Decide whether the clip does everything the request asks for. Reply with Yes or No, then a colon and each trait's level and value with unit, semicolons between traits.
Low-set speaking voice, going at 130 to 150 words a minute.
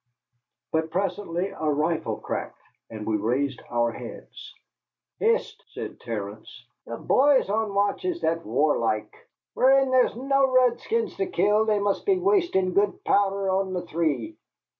No: high, 195 Hz; average, 140 wpm